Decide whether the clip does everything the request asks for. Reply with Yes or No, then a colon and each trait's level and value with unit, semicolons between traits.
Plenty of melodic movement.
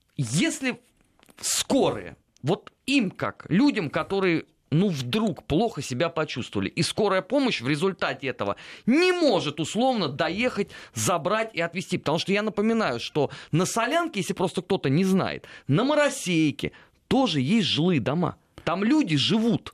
Yes: wide, 6.5 semitones